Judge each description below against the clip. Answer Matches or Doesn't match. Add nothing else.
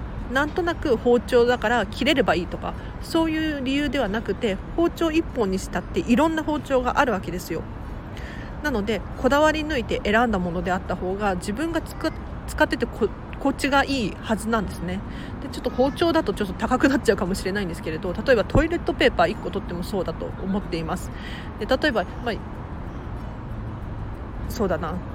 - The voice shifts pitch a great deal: Matches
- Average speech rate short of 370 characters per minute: Doesn't match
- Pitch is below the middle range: Doesn't match